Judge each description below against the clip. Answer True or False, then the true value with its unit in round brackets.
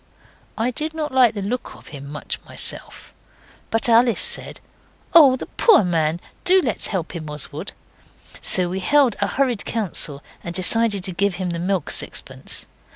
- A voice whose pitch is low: False (200 Hz)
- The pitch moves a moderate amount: False (6.3 semitones)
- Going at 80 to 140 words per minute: False (165 wpm)